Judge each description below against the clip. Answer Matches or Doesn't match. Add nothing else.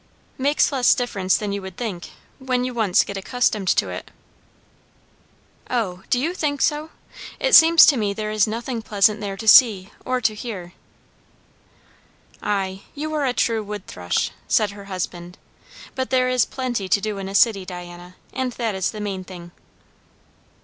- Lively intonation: Doesn't match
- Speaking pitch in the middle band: Doesn't match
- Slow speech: Doesn't match